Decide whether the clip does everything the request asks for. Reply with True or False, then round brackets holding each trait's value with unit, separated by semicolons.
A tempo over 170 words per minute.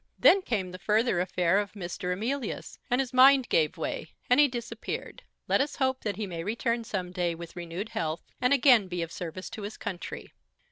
True (200 wpm)